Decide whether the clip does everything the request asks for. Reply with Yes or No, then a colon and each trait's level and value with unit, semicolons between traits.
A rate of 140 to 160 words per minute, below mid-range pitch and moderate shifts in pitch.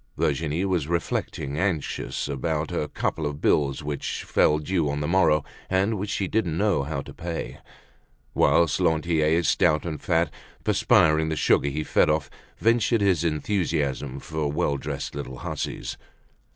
Yes: average, 150 wpm; very low, 80 Hz; average, 3.1 semitones